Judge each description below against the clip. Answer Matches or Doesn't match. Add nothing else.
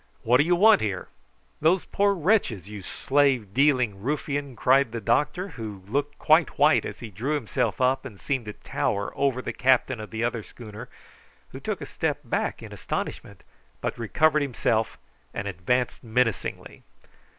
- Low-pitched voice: Matches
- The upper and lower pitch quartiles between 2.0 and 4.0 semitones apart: Doesn't match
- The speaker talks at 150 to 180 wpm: Matches